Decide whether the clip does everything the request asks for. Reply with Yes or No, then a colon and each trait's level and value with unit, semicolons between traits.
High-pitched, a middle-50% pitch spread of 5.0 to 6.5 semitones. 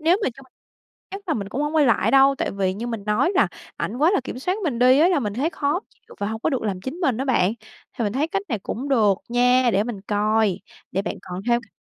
Yes: high, 245 Hz; average, 5.3 semitones